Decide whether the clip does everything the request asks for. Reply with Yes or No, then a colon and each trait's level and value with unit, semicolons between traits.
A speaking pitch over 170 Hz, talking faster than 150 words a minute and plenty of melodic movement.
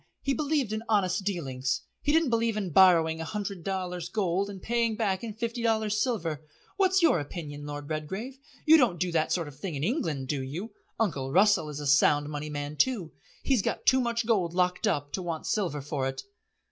Yes: medium, 185 Hz; fast, 205 wpm; wide, 6.8 semitones